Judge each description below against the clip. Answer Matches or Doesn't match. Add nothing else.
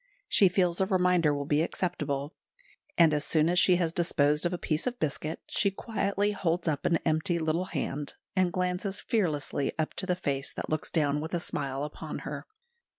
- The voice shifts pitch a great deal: Doesn't match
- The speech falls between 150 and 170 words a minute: Doesn't match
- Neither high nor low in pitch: Matches